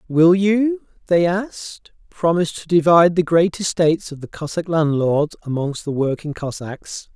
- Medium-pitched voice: Yes, medium, 165 Hz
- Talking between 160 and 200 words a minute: No, average, 150 wpm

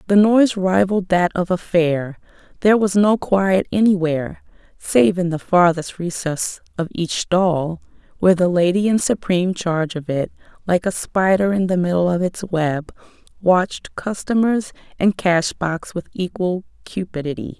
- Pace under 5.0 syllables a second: Yes, 4.6 syllables/s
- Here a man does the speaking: No, female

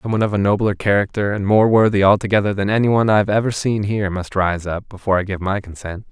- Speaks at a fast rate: Yes, fast, 235 wpm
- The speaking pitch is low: Yes, low, 100 Hz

